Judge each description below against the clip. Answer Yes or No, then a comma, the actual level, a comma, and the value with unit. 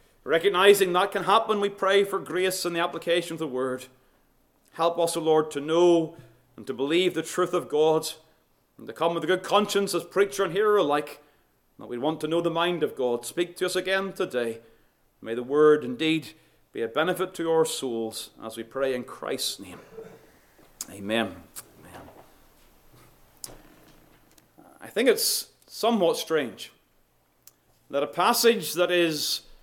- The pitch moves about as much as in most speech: No, wide, 5.7 semitones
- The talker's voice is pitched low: No, medium, 165 Hz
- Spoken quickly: No, average, 165 wpm